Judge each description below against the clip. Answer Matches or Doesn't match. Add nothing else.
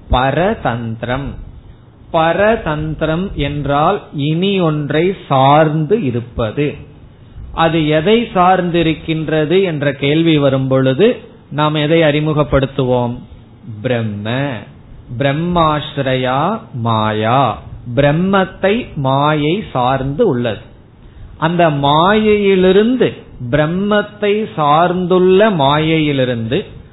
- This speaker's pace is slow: Matches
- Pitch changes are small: Doesn't match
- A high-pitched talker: Doesn't match